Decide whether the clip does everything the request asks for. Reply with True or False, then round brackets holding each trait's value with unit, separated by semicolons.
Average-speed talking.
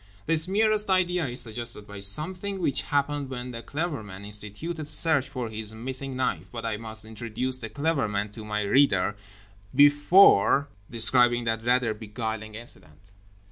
True (155 wpm)